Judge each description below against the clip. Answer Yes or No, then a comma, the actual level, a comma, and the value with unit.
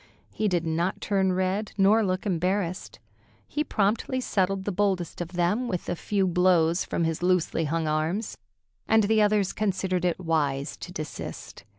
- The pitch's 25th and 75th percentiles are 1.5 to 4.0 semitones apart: Yes, average, 3.2 semitones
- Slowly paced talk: No, average, 165 wpm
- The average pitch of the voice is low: No, medium, 185 Hz